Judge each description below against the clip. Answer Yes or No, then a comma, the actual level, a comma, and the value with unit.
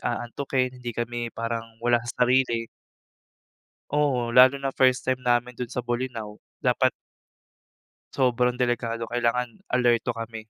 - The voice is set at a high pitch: No, low, 120 Hz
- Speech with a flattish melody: Yes, narrow, 1.4 semitones